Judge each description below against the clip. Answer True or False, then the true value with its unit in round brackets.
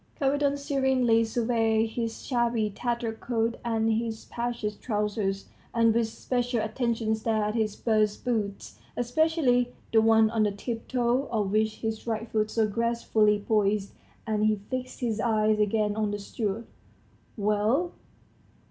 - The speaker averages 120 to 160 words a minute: True (140 wpm)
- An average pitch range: False (2.0 semitones)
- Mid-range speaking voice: False (225 Hz)